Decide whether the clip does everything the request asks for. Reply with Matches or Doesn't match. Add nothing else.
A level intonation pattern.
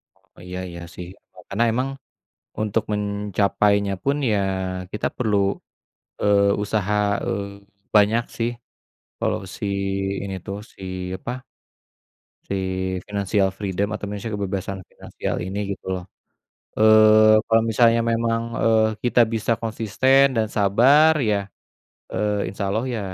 Matches